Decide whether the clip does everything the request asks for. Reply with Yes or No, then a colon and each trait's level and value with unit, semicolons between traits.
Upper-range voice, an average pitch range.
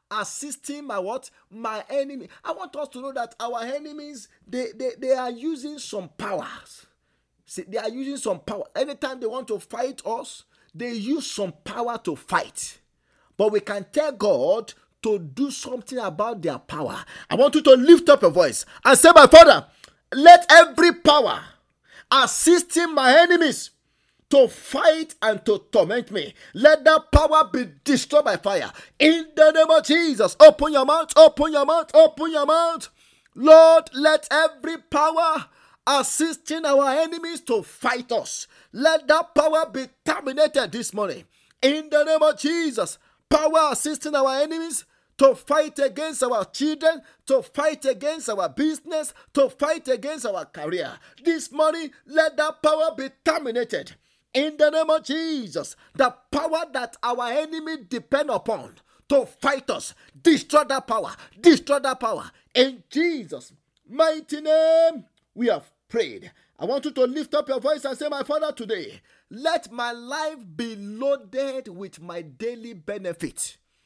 Yes: very high, 285 Hz; average, 4.1 semitones